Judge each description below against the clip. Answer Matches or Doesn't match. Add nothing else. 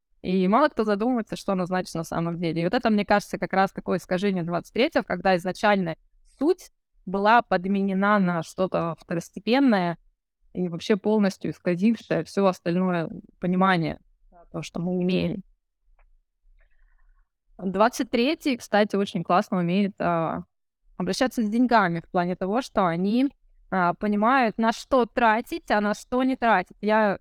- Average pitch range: Matches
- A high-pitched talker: Matches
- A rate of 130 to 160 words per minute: Matches